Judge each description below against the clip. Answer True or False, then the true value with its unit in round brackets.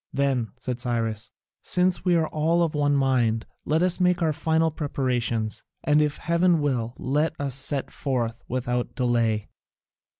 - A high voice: False (140 Hz)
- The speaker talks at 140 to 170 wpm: True (155 wpm)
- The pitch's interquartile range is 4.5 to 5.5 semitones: True (4.8 semitones)